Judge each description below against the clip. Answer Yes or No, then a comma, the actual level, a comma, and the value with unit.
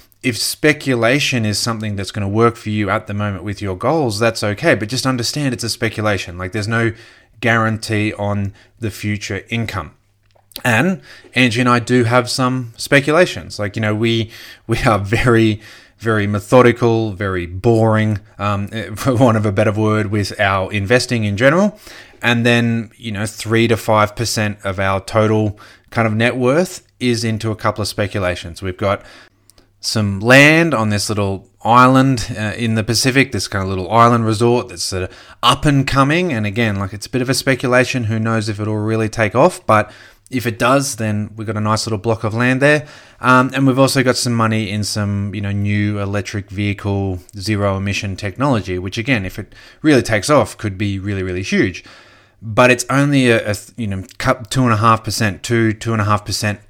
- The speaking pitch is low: Yes, low, 110 Hz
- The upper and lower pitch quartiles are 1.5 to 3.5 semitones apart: Yes, average, 2.9 semitones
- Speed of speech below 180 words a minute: No, average, 195 wpm